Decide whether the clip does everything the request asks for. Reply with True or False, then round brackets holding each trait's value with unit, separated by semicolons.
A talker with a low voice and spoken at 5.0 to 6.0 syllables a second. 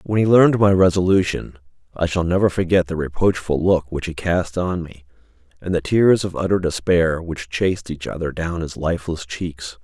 True (90 Hz; 5.1 syllables/s)